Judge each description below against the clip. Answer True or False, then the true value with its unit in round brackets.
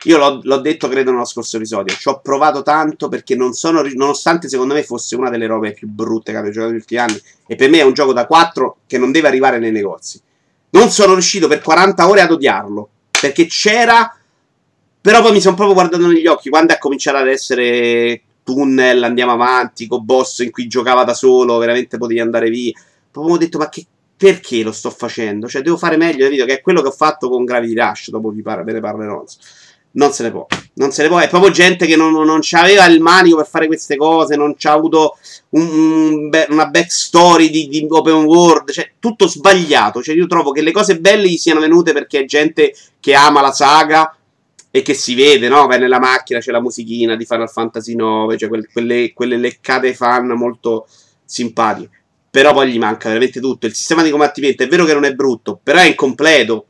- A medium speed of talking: False (215 wpm)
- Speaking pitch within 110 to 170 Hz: True (140 Hz)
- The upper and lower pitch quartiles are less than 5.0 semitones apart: False (5.4 semitones)